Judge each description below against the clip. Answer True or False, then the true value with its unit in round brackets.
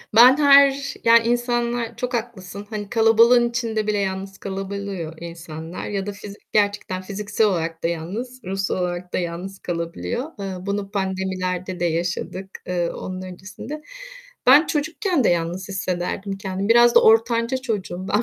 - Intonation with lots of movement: False (4.1 semitones)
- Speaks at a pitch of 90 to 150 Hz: False (200 Hz)